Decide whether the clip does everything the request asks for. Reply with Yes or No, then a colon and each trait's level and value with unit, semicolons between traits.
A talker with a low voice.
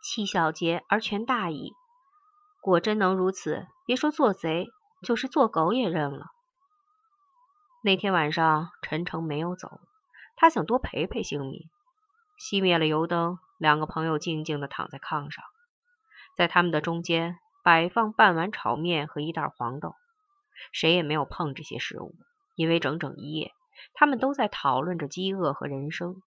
No: medium, 180 Hz